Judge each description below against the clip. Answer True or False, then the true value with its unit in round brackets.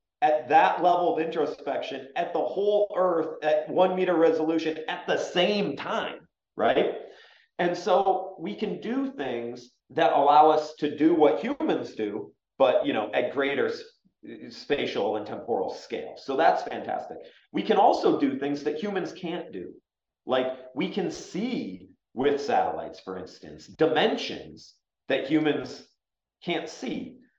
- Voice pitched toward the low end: False (175 Hz)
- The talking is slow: False (145 wpm)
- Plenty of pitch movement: True (8.9 semitones)